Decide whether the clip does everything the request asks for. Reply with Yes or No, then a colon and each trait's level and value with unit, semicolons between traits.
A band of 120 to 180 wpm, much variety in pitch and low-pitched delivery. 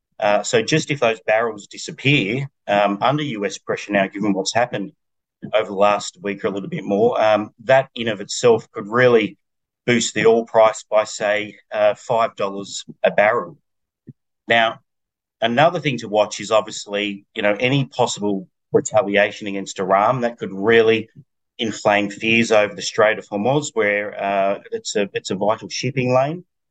No: average, 165 wpm; average, 3.6 semitones; low, 110 Hz